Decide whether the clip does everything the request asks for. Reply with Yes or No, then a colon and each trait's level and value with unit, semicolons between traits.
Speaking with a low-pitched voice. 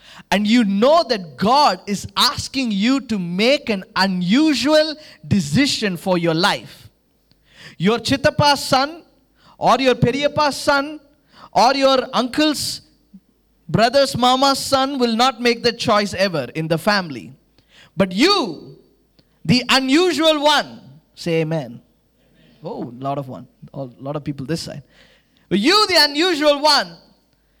No: high, 240 Hz